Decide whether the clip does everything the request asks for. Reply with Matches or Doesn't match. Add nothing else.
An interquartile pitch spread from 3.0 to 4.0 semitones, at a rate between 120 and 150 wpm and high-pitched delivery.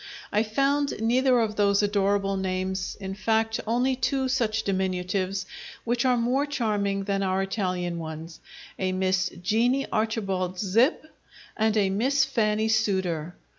Matches